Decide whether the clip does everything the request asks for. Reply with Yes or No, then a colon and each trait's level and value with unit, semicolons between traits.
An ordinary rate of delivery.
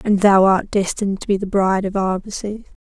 No: fast, 210 wpm